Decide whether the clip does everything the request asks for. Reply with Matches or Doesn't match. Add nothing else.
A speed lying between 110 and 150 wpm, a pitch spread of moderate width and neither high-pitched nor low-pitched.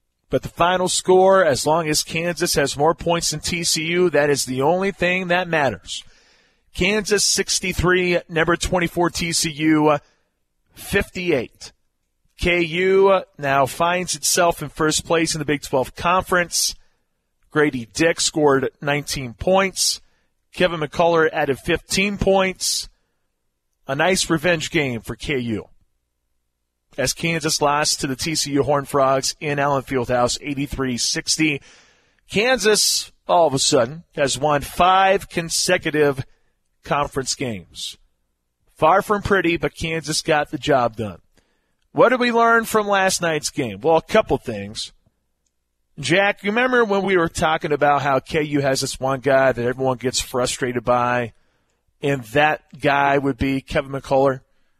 Matches